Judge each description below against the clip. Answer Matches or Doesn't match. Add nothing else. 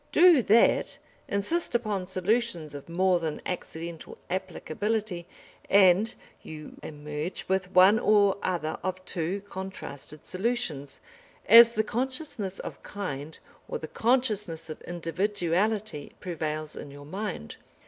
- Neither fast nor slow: Doesn't match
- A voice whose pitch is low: Doesn't match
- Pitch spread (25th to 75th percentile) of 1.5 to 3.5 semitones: Doesn't match